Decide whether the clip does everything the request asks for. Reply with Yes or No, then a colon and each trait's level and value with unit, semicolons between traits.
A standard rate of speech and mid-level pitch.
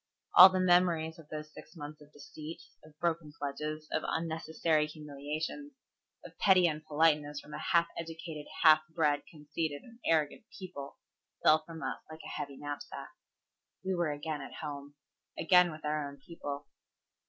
Yes: average, 155 wpm; medium, 155 Hz